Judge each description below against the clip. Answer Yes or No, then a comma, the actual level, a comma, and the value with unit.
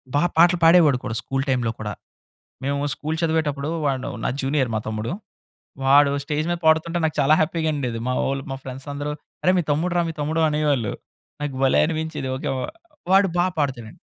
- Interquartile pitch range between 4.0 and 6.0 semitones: No, average, 3.0 semitones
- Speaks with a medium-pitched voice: Yes, medium, 145 Hz